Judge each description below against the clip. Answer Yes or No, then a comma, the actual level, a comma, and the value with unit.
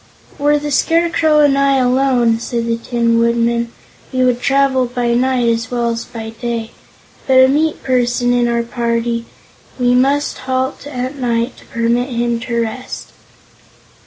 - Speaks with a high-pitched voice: Yes, high, 245 Hz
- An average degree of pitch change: No, narrow, 2.2 semitones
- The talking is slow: No, average, 160 wpm